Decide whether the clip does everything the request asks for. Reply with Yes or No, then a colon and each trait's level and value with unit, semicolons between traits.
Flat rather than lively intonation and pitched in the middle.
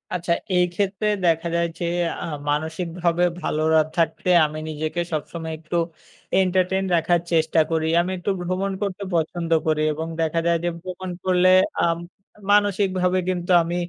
Yes: narrow, 2.3 semitones; medium, 175 Hz